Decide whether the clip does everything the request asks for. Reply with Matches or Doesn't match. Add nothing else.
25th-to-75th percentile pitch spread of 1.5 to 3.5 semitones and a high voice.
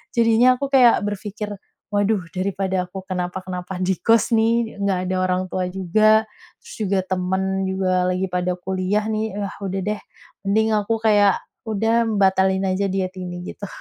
Matches